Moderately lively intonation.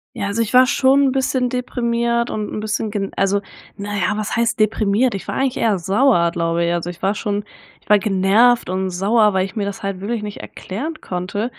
Yes: average, 3.5 semitones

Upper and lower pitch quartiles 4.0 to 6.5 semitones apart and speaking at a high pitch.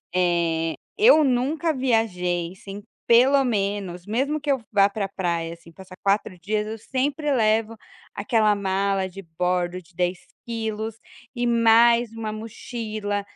Yes: average, 4.3 semitones; high, 215 Hz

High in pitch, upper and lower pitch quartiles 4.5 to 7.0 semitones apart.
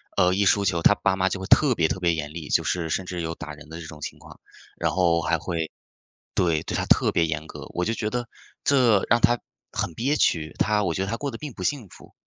No: very low, 90 Hz; average, 5.0 semitones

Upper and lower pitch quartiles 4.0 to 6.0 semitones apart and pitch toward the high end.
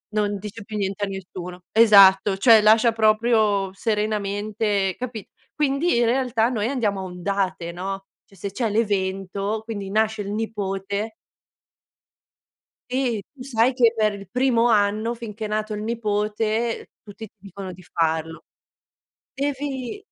No: average, 2.7 semitones; high, 210 Hz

